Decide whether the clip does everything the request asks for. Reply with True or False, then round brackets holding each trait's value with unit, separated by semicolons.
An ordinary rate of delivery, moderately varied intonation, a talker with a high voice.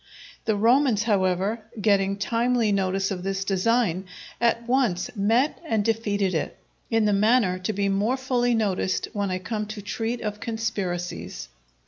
True (150 wpm; 3.0 semitones; 210 Hz)